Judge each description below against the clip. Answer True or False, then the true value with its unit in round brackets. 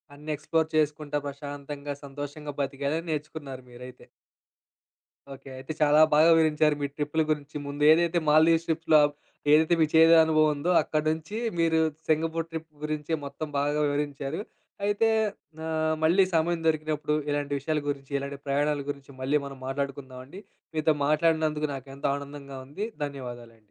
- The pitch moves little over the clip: True (2.0 semitones)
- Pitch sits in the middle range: True (150 Hz)